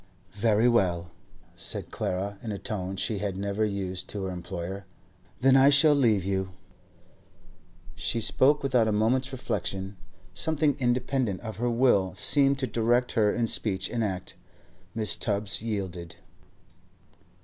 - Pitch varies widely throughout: No, average, 4.3 semitones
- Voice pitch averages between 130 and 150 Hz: No, low, 105 Hz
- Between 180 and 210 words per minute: No, average, 145 wpm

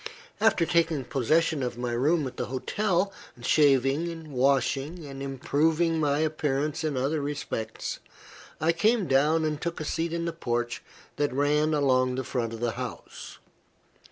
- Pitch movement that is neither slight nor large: Yes, average, 3.8 semitones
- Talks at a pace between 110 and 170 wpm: Yes, average, 155 wpm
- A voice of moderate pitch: Yes, medium, 145 Hz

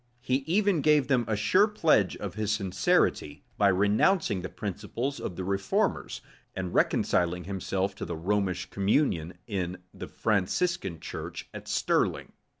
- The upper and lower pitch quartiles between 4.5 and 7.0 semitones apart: Yes, wide, 5.6 semitones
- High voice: No, low, 100 Hz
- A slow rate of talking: No, average, 145 wpm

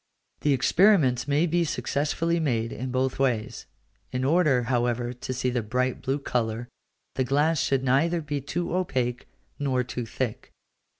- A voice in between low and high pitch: No, low, 130 Hz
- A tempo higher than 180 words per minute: No, average, 155 wpm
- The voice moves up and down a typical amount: Yes, average, 3.3 semitones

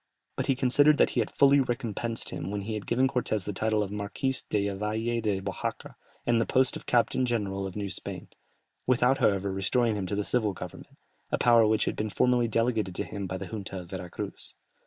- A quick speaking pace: Yes, fast, 220 wpm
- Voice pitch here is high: No, low, 110 Hz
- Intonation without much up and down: No, average, 3.5 semitones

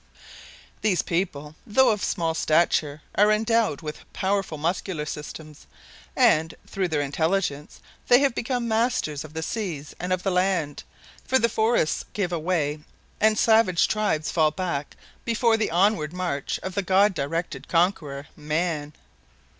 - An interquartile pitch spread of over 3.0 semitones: Yes, wide, 5.5 semitones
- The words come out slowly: No, average, 145 wpm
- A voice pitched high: No, medium, 180 Hz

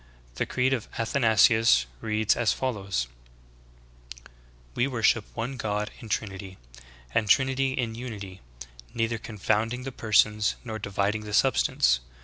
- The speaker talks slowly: Yes, slow, 130 wpm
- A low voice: Yes, low, 110 Hz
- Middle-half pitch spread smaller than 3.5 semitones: Yes, average, 2.9 semitones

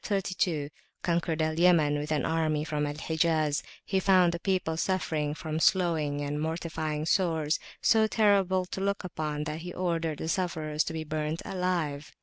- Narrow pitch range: No, average, 3.0 semitones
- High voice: No, medium, 160 Hz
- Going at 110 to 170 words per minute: Yes, average, 165 wpm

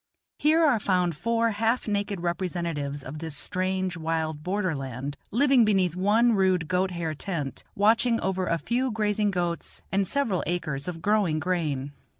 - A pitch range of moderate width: Yes, average, 4.4 semitones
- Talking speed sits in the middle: Yes, average, 155 wpm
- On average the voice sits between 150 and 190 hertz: Yes, medium, 185 Hz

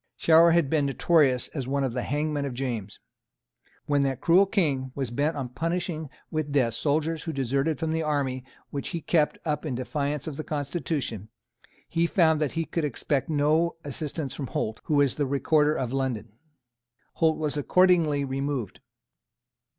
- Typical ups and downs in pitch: Yes, average, 3.0 semitones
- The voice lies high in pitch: No, medium, 145 Hz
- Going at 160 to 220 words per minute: Yes, average, 170 wpm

